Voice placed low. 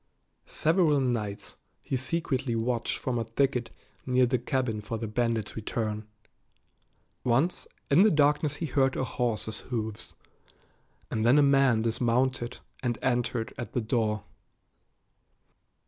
Yes: low, 120 Hz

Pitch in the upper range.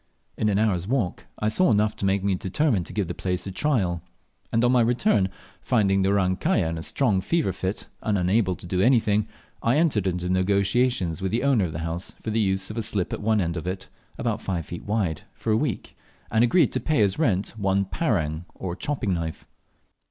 No: low, 100 Hz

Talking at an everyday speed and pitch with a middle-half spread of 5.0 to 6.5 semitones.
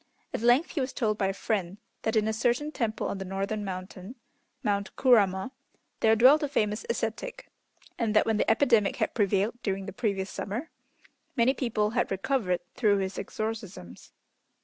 No: average, 170 wpm; average, 3.6 semitones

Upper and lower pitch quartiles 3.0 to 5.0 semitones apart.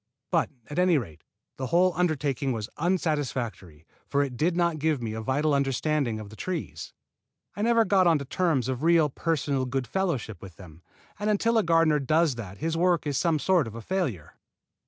No: wide, 5.4 semitones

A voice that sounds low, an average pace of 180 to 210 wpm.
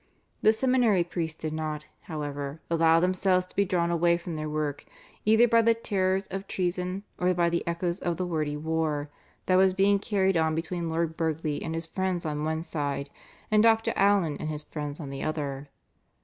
No: medium, 170 Hz; average, 190 wpm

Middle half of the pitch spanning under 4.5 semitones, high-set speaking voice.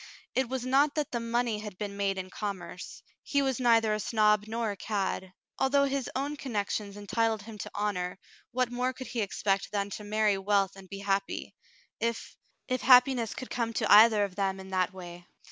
Yes: average, 3.6 semitones; high, 215 Hz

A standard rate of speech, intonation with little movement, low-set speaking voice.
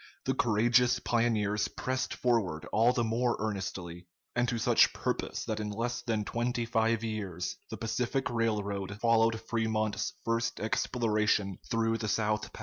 Yes: average, 145 wpm; narrow, 2.0 semitones; low, 115 Hz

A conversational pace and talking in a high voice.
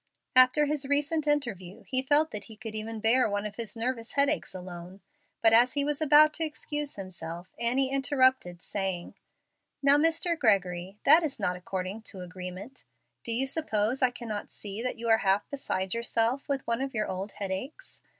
Yes: average, 180 wpm; high, 230 Hz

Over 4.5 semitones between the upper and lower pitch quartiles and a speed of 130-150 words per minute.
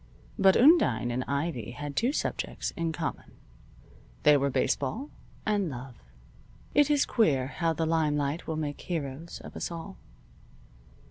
Yes: average, 4.9 semitones; average, 140 wpm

